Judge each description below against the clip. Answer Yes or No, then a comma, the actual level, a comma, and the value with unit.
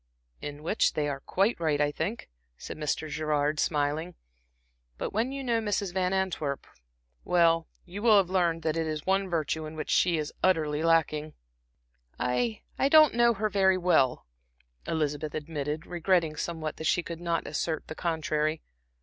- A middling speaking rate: Yes, average, 170 wpm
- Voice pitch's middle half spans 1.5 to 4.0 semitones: Yes, average, 3.6 semitones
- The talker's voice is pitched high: No, medium, 165 Hz